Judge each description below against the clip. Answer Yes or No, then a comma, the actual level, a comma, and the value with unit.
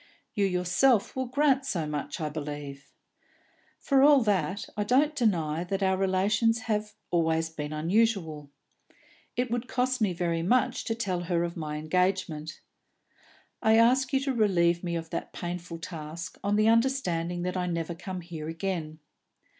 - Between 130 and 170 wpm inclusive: Yes, average, 160 wpm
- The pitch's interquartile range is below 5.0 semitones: No, wide, 5.5 semitones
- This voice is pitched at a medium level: Yes, medium, 180 Hz